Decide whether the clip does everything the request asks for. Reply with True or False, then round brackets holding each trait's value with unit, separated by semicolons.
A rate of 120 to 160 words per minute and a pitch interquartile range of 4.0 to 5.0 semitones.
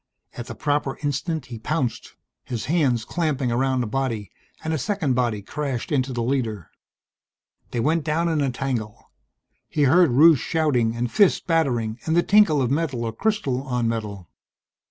False (170 wpm; 4.7 semitones)